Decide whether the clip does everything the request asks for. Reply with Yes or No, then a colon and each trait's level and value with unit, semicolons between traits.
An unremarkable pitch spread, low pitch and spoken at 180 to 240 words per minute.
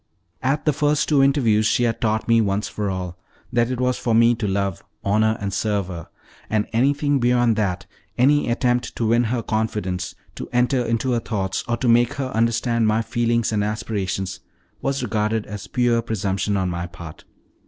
Yes: average, 3.0 semitones; low, 115 Hz; average, 185 wpm